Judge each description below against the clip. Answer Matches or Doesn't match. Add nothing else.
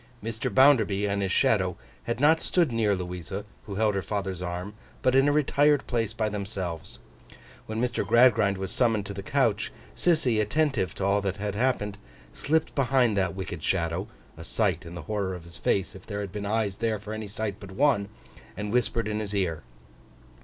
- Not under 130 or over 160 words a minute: Doesn't match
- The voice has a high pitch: Doesn't match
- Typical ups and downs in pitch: Matches